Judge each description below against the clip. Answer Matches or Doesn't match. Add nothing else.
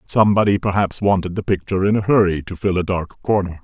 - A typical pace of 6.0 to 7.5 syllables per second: Matches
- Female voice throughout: Doesn't match